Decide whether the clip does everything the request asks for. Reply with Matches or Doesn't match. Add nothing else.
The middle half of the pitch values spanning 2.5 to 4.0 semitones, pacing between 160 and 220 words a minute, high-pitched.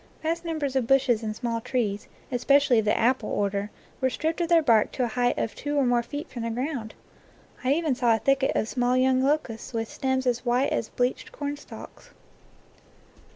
Matches